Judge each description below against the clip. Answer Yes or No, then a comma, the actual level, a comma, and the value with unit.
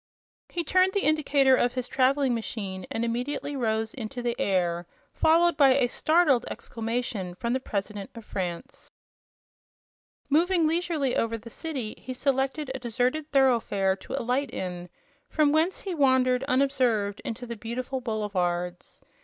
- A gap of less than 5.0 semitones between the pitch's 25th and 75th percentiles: Yes, average, 4.4 semitones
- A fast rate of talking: No, average, 145 wpm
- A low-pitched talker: No, very high, 250 Hz